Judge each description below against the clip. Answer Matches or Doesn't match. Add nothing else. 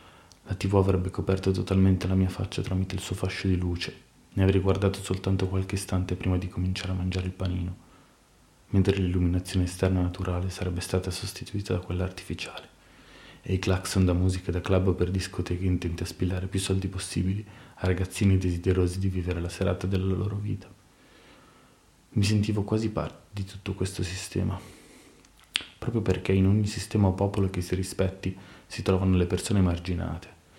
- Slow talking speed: Doesn't match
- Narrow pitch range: Matches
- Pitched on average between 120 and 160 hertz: Doesn't match